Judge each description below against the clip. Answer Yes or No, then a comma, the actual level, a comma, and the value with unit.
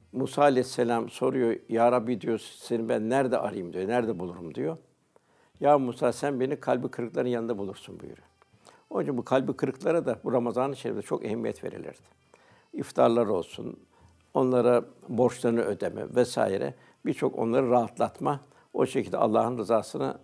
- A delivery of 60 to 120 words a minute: No, fast, 140 wpm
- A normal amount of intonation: No, narrow, 1.8 semitones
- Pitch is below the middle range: Yes, low, 125 Hz